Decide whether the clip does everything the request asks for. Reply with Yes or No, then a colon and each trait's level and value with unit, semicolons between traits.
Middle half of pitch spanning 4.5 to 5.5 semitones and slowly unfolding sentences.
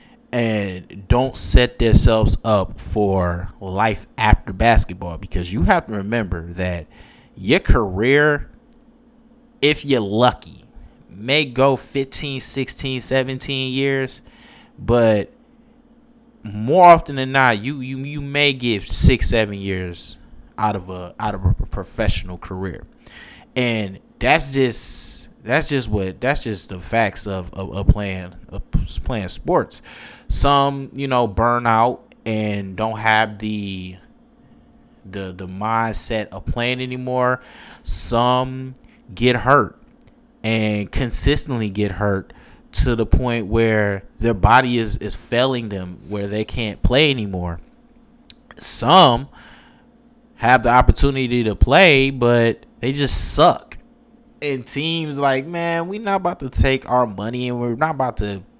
Yes: average, 5.1 semitones; slow, 130 wpm